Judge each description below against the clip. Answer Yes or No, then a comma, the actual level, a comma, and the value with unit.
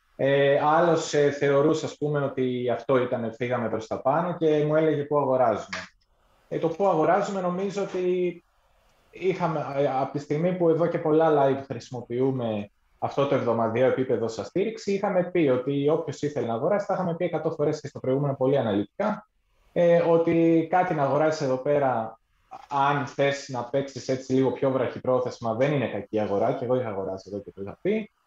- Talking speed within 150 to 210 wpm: Yes, fast, 170 wpm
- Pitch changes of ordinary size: Yes, average, 4.3 semitones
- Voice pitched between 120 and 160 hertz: Yes, medium, 140 Hz